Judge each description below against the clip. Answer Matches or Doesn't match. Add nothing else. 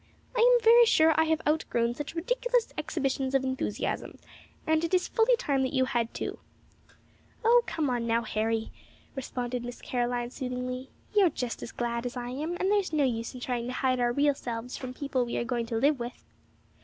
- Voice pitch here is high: Matches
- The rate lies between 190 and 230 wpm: Matches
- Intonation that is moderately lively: Matches